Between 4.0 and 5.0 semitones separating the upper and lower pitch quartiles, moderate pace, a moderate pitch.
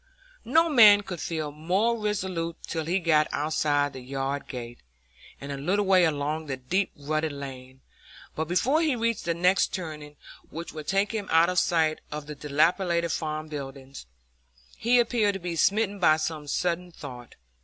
Yes: average, 4.7 semitones; average, 170 wpm; medium, 165 Hz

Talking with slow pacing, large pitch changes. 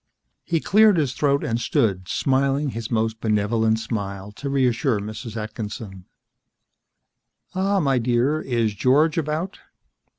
No: slow, 125 wpm; average, 4.7 semitones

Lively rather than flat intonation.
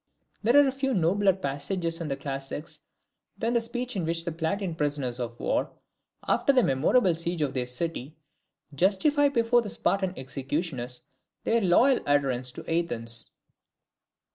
Yes: wide, 7.5 semitones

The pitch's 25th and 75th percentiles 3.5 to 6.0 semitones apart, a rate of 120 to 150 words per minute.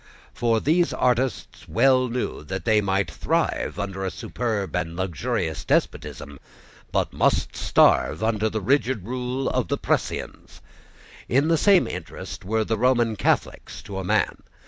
Yes: average, 4.8 semitones; average, 145 wpm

